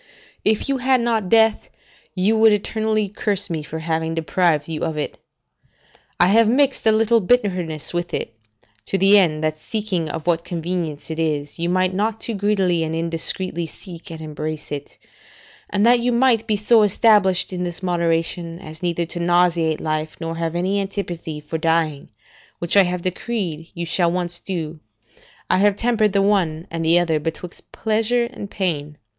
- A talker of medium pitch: Yes, medium, 175 Hz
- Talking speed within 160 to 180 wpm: Yes, average, 175 wpm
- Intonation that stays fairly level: No, average, 4.2 semitones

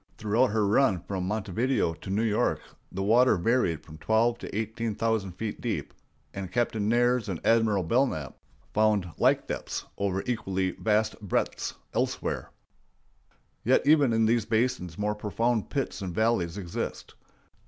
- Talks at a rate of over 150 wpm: No, average, 145 wpm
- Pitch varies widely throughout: No, average, 3.3 semitones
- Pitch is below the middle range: Yes, low, 110 Hz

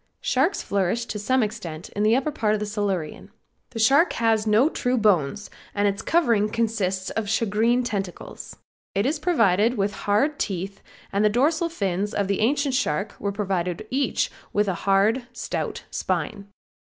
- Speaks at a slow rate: No, average, 165 wpm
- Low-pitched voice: No, high, 210 Hz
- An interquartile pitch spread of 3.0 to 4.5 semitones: Yes, average, 3.5 semitones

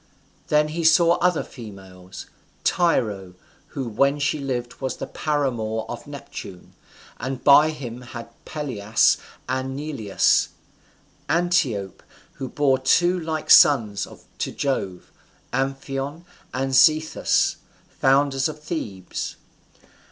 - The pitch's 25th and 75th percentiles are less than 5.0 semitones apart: Yes, average, 4.6 semitones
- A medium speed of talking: No, slow, 105 wpm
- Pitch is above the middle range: No, low, 135 Hz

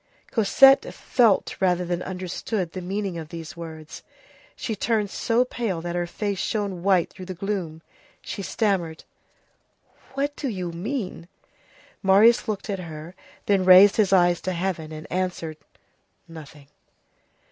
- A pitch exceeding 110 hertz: Yes, medium, 185 Hz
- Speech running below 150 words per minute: Yes, average, 140 wpm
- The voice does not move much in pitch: No, average, 3.3 semitones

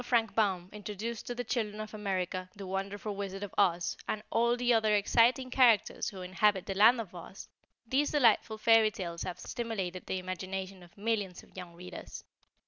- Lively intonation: No, average, 3.4 semitones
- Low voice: No, high, 205 Hz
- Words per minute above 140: Yes, average, 180 wpm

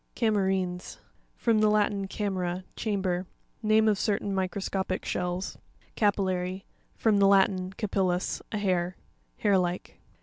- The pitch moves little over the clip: Yes, narrow, 2.0 semitones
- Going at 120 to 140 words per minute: Yes, slow, 135 wpm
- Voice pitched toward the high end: Yes, high, 195 Hz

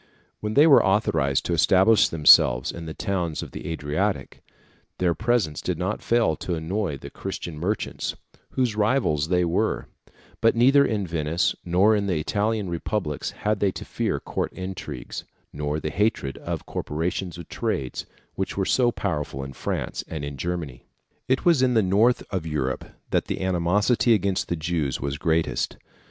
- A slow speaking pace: No, average, 170 wpm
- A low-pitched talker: Yes, very low, 90 Hz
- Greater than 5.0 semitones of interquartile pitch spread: Yes, wide, 5.4 semitones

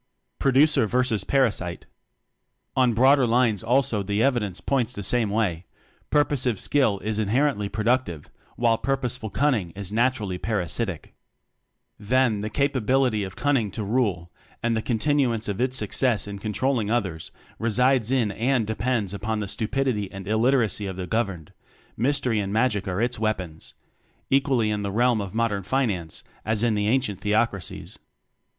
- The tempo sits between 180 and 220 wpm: No, average, 155 wpm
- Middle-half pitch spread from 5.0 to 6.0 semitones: No, average, 3.9 semitones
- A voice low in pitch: Yes, low, 110 Hz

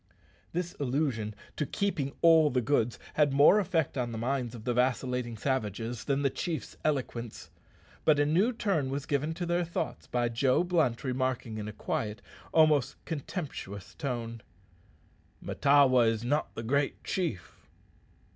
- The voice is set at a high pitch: No, low, 135 Hz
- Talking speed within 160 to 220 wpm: No, average, 150 wpm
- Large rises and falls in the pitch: No, average, 4.6 semitones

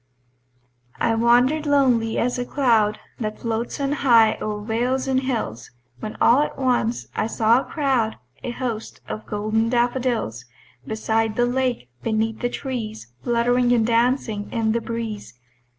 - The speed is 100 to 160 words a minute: Yes, average, 150 wpm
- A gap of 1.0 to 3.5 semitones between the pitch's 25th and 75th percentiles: Yes, narrow, 2.4 semitones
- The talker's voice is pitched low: No, high, 235 Hz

